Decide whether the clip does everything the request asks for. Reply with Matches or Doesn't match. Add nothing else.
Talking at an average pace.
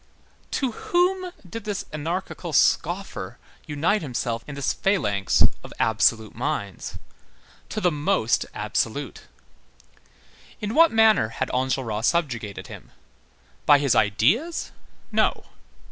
Doesn't match